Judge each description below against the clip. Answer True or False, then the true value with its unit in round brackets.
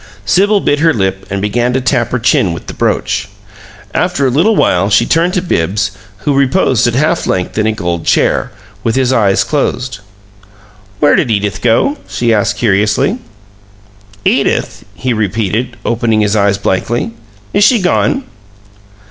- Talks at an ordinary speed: True (160 wpm)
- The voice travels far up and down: True (5.7 semitones)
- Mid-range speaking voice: False (120 Hz)